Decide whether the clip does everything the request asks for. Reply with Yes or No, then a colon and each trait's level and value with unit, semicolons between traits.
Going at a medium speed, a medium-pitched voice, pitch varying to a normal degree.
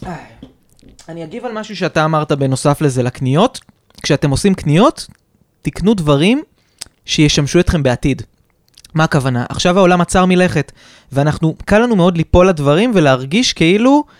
Yes: average, 130 wpm; medium, 165 Hz; average, 4.9 semitones